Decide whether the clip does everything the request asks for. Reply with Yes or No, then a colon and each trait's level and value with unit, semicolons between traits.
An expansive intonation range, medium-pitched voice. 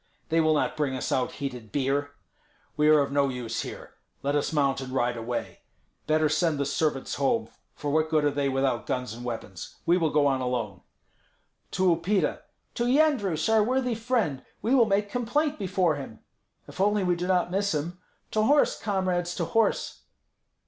Yes: wide, 6.5 semitones; medium, 155 Hz